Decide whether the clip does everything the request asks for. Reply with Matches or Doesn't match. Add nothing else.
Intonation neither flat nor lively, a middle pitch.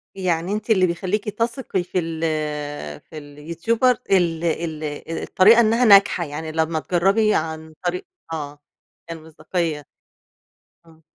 Matches